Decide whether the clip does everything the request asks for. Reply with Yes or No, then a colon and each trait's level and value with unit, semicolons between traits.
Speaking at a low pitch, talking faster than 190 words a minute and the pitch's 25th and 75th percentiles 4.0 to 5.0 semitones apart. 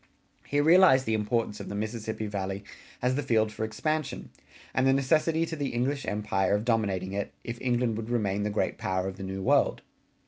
Yes: low, 110 Hz; average, 200 wpm; average, 4.5 semitones